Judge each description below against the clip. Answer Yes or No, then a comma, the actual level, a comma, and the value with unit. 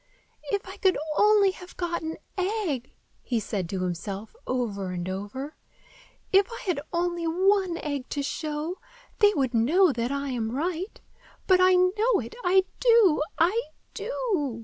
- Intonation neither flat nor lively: No, wide, 7.2 semitones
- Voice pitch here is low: No, very high, 335 Hz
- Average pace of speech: Yes, average, 155 wpm